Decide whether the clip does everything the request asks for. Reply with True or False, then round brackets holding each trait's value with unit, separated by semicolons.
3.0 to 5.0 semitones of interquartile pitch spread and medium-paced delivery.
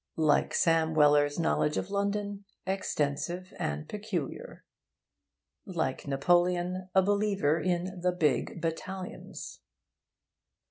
False (3.7 semitones; 95 wpm)